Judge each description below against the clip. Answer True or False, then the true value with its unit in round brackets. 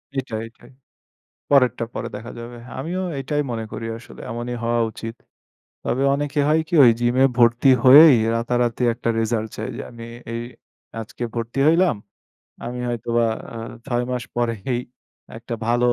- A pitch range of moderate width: False (2.2 semitones)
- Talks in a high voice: False (120 Hz)